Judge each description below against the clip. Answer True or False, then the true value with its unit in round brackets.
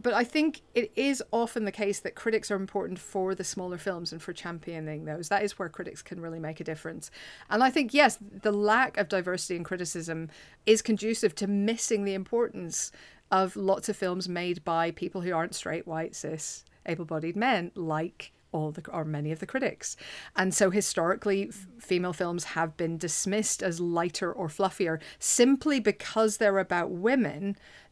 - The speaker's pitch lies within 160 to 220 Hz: True (190 Hz)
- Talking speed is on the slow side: False (180 wpm)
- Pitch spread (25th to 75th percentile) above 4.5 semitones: False (3.9 semitones)